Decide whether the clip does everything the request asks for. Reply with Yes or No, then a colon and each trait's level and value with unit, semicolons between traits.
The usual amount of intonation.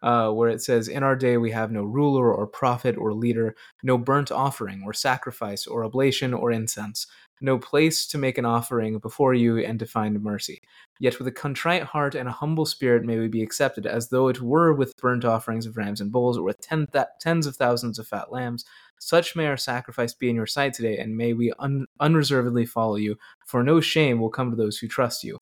Yes: average, 3.1 semitones